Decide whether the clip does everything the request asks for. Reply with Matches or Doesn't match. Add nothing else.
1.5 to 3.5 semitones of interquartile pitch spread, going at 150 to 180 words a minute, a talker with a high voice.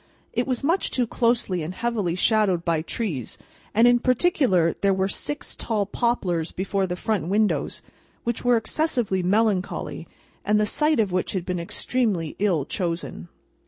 Doesn't match